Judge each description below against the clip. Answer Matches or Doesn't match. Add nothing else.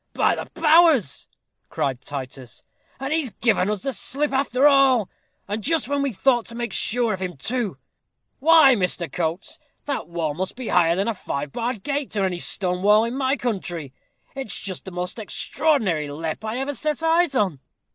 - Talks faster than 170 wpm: Matches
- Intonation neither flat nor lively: Doesn't match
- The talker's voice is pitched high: Matches